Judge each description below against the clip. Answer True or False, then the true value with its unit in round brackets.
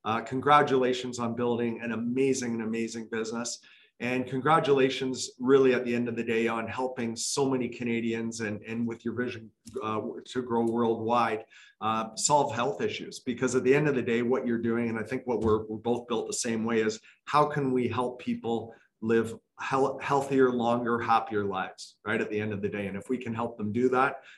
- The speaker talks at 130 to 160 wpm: False (205 wpm)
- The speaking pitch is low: True (120 Hz)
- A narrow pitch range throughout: True (2.1 semitones)